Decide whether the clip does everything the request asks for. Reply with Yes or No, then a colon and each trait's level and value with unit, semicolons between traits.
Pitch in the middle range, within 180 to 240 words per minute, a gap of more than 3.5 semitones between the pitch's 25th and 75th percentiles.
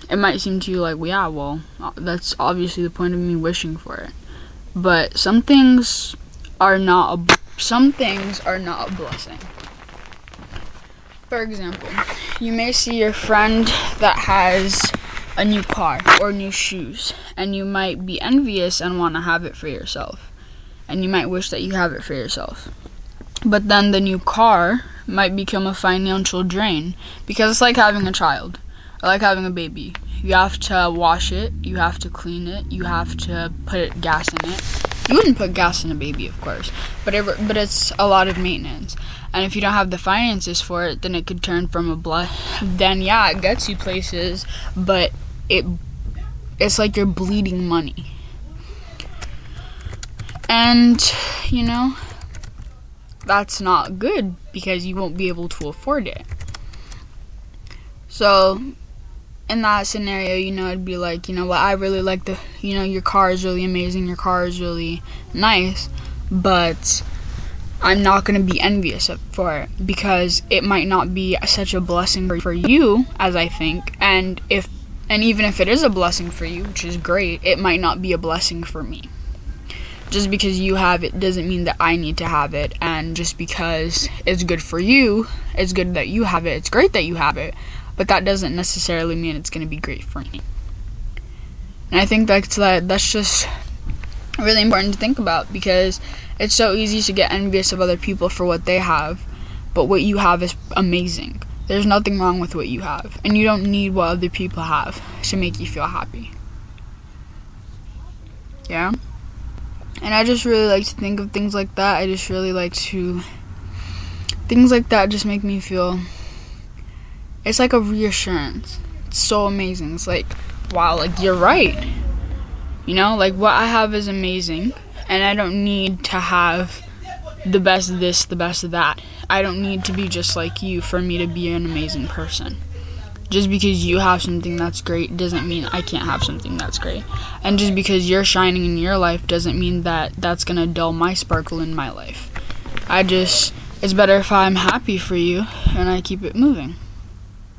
Yes: medium, 180 Hz; average, 185 wpm; average, 4.2 semitones